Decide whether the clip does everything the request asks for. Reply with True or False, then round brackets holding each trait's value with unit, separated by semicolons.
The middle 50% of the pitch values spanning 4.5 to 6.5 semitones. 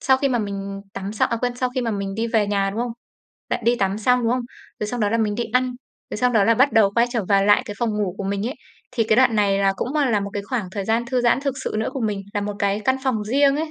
False (3.6 semitones)